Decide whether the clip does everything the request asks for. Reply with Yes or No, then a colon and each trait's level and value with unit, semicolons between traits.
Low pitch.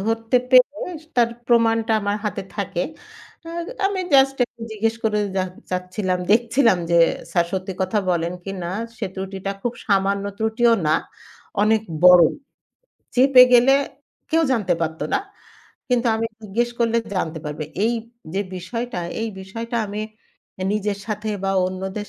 No: high, 215 Hz